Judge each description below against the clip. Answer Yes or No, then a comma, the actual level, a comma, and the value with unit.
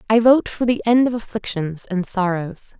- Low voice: No, high, 210 Hz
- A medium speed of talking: Yes, average, 195 wpm